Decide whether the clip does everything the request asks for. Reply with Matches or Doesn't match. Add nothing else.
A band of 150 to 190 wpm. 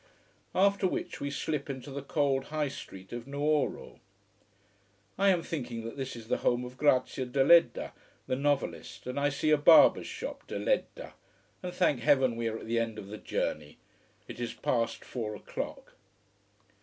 Matches